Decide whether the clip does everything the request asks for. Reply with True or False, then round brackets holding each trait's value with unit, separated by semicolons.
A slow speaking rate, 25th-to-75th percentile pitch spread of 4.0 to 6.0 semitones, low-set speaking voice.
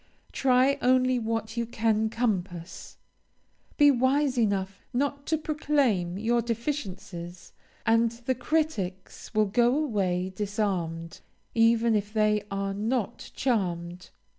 False (115 wpm; 4.5 semitones; 225 Hz)